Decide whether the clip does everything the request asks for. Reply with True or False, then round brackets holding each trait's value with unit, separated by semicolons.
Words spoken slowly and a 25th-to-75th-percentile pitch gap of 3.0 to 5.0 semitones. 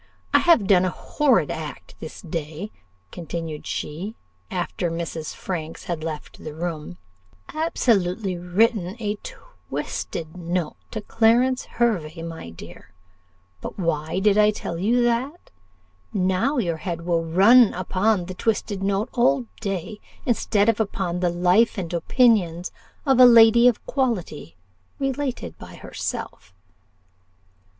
False (130 wpm; 5.5 semitones)